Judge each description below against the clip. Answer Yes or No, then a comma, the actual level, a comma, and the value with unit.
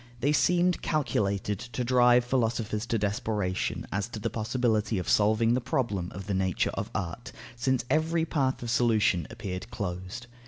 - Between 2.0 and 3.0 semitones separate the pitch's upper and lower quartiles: No, average, 3.9 semitones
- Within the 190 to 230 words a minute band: No, average, 160 wpm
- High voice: No, low, 115 Hz